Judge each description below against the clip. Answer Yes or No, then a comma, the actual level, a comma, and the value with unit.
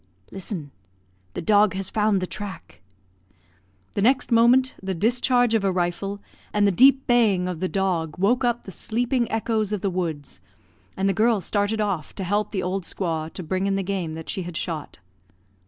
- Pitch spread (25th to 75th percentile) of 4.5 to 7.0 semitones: No, average, 3.5 semitones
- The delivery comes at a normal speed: Yes, average, 190 wpm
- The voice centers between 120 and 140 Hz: No, high, 195 Hz